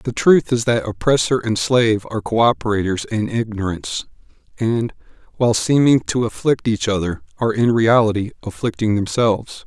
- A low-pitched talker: Yes, low, 115 Hz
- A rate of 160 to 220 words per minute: No, average, 150 wpm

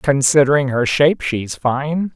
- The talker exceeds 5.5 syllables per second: No, 4.3 syllables/s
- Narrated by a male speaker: Yes, male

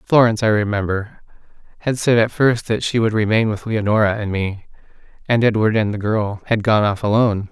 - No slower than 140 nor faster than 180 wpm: No, average, 190 wpm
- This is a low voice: Yes, low, 110 Hz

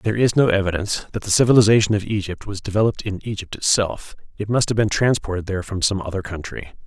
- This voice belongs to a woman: No, male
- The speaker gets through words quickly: Yes, fast, 210 wpm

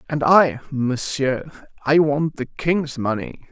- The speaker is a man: Yes, male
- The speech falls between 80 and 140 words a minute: Yes, slow, 135 wpm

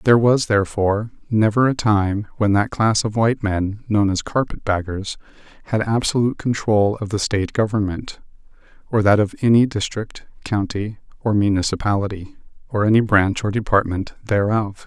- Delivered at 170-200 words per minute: No, average, 150 wpm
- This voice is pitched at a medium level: No, low, 105 Hz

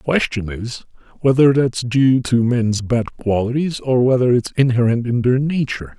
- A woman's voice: No, male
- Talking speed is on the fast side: No, average, 170 wpm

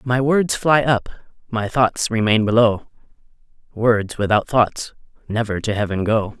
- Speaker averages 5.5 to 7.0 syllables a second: No, 4.1 syllables/s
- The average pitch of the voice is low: Yes, low, 110 Hz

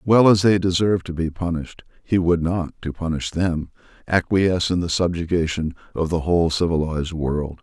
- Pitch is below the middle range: Yes, very low, 85 Hz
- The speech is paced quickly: No, average, 175 wpm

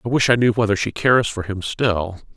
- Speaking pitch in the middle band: No, low, 110 Hz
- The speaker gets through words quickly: Yes, fast, 255 wpm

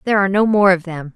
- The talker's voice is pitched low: No, high, 190 Hz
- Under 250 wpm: No, fast, 310 wpm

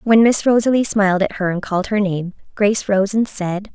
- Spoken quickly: Yes, fast, 225 wpm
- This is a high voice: Yes, high, 205 Hz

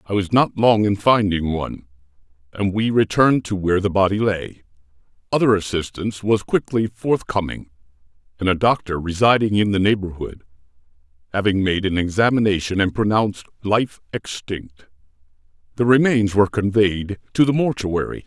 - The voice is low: Yes, low, 100 Hz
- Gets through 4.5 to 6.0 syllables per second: Yes, 5.3 syllables/s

